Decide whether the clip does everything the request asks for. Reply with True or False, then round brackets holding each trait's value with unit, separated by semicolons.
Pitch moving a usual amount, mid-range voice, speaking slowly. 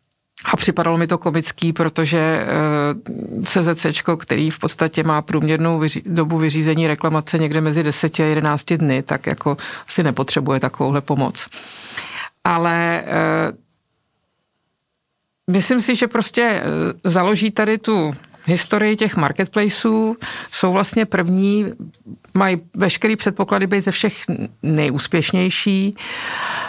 True (4.4 semitones; 170 Hz; 110 wpm)